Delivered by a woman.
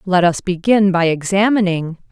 Yes: female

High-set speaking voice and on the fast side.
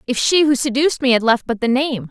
Yes: very high, 260 Hz; fast, 285 wpm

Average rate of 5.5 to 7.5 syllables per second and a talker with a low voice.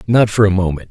Yes: 6.5 syllables/s; low, 100 Hz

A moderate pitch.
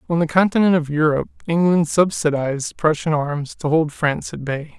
Yes: medium, 155 Hz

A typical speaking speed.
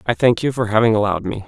No: fast, 285 wpm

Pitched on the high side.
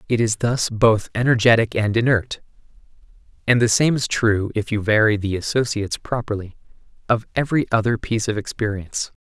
No: low, 110 Hz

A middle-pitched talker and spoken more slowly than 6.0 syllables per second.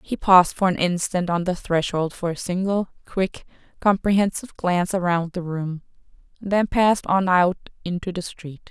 Yes: medium, 180 Hz; 5.0 syllables/s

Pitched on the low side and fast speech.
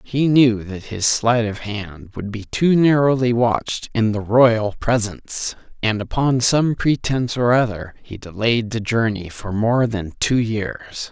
No: low, 115 Hz; average, 165 wpm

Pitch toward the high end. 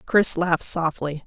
No: medium, 170 Hz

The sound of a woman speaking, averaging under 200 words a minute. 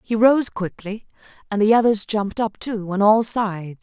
Yes: female; average, 190 wpm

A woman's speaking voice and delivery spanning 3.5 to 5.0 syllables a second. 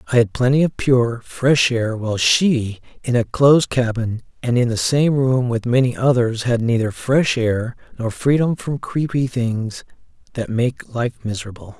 No: male; 4.5 syllables/s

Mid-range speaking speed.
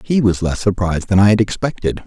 No: fast, 235 wpm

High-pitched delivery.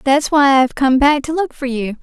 Yes: very high, 275 Hz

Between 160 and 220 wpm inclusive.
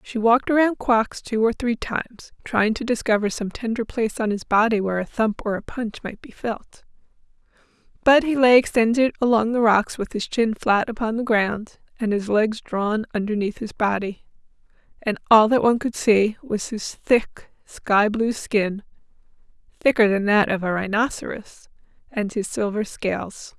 Yes: average, 170 wpm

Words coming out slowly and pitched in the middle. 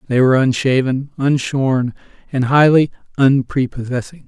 No: slow, 100 wpm; low, 130 Hz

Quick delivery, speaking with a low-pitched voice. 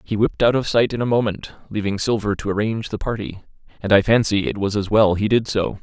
Yes: fast, 245 wpm; low, 105 Hz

